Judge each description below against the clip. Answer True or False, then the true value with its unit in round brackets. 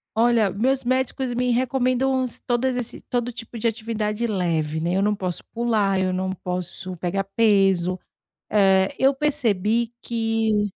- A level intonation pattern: False (4.1 semitones)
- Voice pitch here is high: True (220 Hz)